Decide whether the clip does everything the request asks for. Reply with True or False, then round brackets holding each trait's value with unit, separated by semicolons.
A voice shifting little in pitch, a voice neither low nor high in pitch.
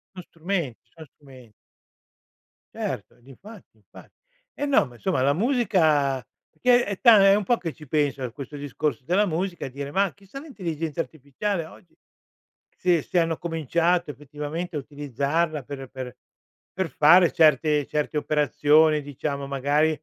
False (4.2 semitones; 155 Hz)